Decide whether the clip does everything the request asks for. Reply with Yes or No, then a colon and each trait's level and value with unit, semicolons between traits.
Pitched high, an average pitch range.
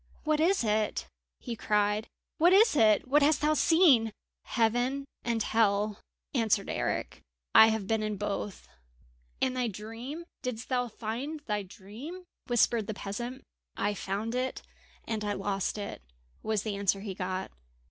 Yes: high, 225 Hz; average, 3.8 semitones